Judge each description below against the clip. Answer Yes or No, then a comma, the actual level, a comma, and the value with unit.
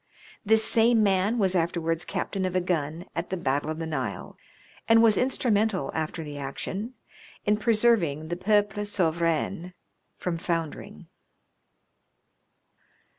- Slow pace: Yes, slow, 125 wpm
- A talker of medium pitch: Yes, medium, 180 Hz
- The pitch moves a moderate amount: Yes, average, 4.6 semitones